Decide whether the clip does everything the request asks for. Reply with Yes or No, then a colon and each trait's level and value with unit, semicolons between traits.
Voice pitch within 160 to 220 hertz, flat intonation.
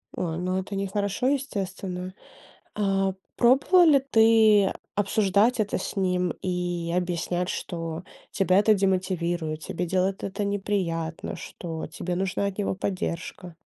Yes: high, 190 Hz; narrow, 2.3 semitones